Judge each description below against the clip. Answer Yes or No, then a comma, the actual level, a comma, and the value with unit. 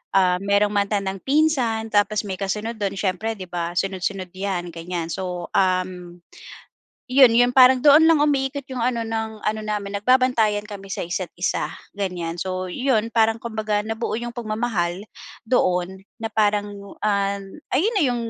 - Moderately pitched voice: No, high, 210 Hz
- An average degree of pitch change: Yes, average, 3.6 semitones